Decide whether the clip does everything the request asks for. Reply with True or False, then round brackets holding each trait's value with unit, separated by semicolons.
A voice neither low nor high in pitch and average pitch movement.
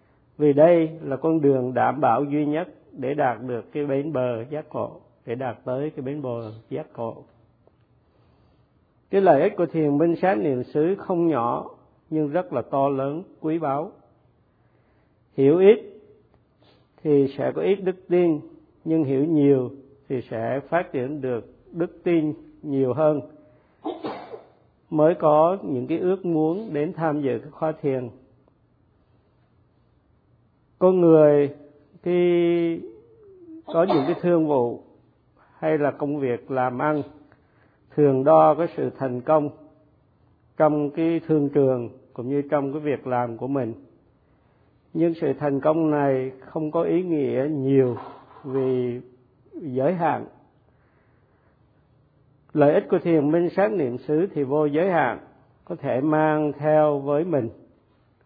True (145 Hz; 3.7 semitones)